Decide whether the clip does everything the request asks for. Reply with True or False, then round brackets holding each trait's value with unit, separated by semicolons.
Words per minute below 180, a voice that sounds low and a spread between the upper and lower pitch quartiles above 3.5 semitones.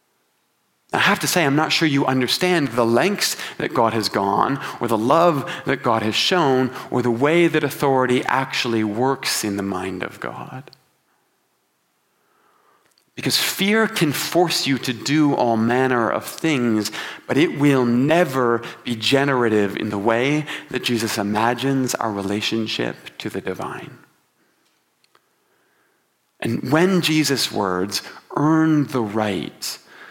True (140 wpm; 130 Hz; 5.4 semitones)